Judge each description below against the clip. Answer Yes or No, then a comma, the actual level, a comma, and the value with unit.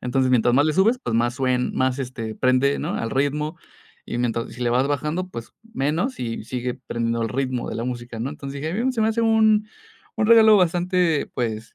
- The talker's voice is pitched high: No, low, 135 Hz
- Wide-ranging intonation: Yes, wide, 6.6 semitones